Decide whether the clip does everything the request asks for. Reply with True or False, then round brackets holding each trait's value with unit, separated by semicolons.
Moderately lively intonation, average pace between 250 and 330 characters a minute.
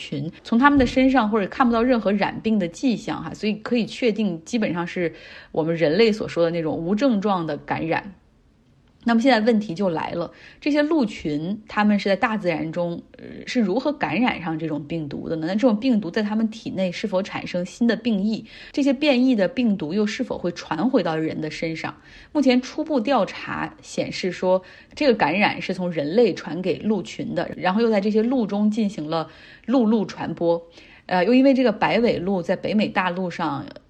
False (6.1 semitones; 295 characters per minute)